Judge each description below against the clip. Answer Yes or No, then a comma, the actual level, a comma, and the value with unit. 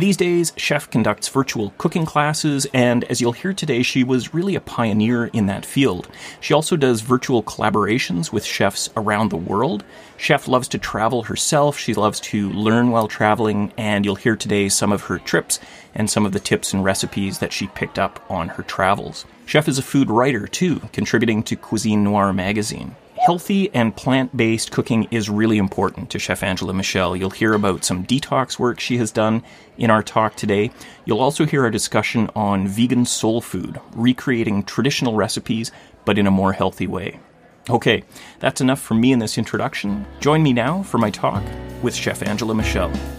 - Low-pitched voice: Yes, low, 110 Hz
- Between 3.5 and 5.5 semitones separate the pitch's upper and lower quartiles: Yes, average, 4.2 semitones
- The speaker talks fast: No, average, 190 wpm